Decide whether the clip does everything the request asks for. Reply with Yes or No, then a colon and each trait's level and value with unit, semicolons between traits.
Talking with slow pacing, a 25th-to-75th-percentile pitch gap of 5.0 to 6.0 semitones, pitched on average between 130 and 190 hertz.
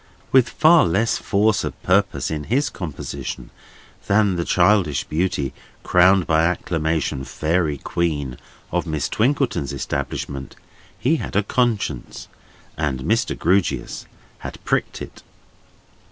No: slow, 120 wpm; wide, 5.6 semitones; very low, 90 Hz